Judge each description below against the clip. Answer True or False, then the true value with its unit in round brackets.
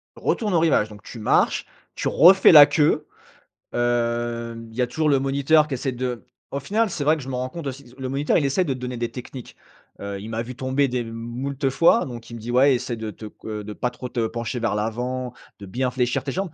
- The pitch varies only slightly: False (3.1 semitones)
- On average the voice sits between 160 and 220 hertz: False (125 Hz)